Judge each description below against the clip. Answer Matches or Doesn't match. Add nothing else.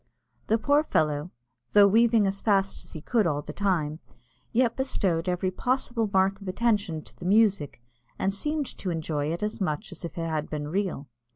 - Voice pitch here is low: Doesn't match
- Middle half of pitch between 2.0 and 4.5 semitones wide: Doesn't match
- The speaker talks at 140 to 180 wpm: Doesn't match